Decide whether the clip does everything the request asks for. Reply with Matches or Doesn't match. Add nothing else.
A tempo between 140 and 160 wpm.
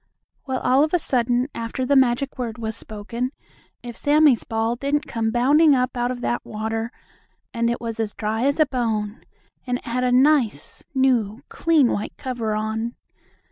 Doesn't match